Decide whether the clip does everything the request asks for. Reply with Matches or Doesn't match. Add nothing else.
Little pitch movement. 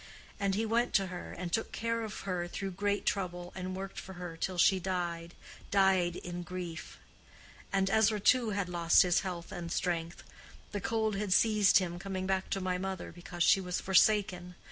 Matches